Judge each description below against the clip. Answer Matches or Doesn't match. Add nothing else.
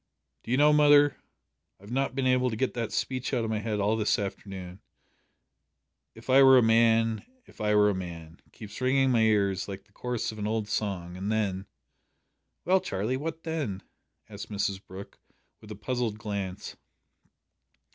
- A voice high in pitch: Doesn't match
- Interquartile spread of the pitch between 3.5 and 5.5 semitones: Matches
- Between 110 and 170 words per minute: Doesn't match